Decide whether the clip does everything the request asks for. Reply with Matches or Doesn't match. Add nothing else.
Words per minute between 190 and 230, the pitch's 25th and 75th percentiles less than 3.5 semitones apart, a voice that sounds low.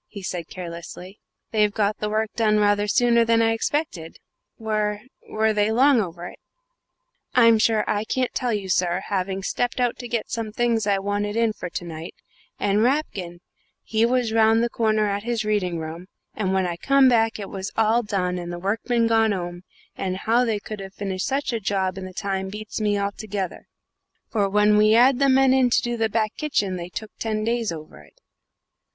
Doesn't match